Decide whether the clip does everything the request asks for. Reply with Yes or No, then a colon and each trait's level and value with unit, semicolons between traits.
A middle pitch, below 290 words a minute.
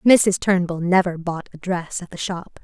Yes: medium, 180 Hz; fast, 205 wpm